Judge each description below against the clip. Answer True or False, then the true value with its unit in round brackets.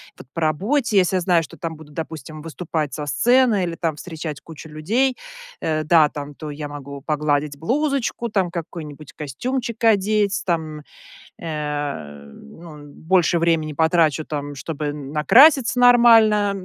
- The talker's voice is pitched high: False (160 Hz)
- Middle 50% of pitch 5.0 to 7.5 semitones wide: True (5.3 semitones)